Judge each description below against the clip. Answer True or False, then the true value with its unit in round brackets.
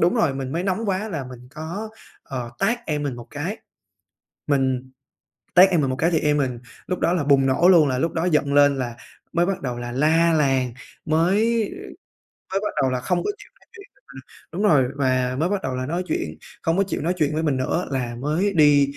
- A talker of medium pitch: True (150 Hz)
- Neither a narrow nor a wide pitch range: True (5.0 semitones)